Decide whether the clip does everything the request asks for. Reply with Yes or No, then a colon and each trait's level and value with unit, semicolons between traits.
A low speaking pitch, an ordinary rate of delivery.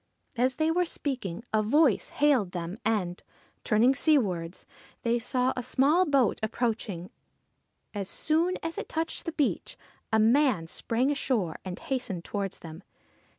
No: high, 240 Hz; average, 150 wpm